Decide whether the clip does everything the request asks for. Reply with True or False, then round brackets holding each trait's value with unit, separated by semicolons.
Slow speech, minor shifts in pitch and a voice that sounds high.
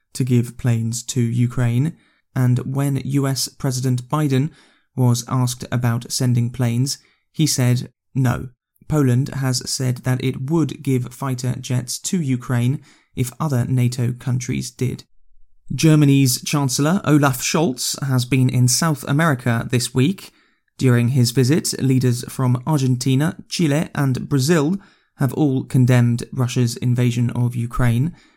False (130 wpm; 2.3 semitones; 130 Hz)